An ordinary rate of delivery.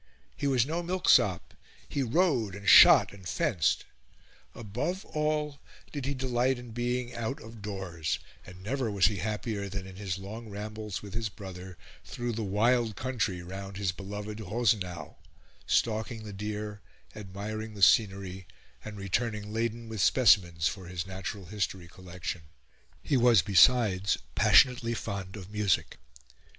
Yes: average, 145 wpm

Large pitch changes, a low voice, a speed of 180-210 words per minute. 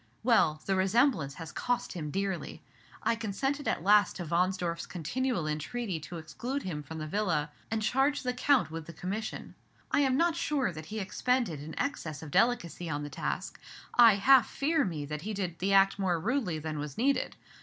No: wide, 7.4 semitones; high, 190 Hz; average, 190 wpm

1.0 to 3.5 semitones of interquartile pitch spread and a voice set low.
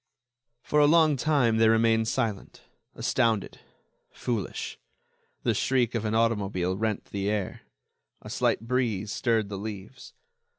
Yes: average, 3.1 semitones; low, 115 Hz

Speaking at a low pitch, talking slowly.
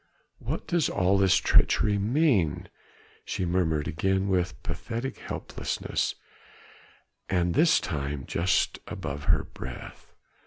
Yes: very low, 95 Hz; slow, 110 wpm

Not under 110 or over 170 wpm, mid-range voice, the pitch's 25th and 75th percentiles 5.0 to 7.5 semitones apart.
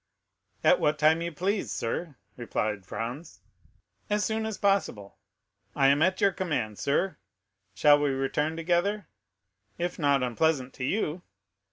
Yes: average, 140 wpm; medium, 155 Hz; wide, 5.6 semitones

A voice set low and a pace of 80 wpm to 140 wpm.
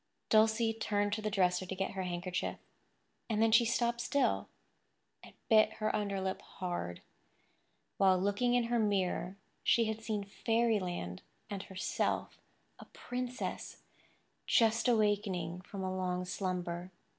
No: high, 205 Hz; slow, 135 wpm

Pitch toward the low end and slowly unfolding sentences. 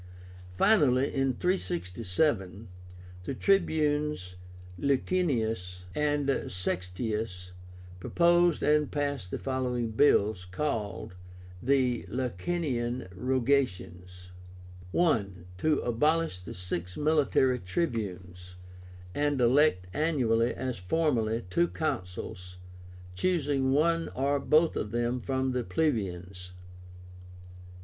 Yes: low, 125 Hz; slow, 90 wpm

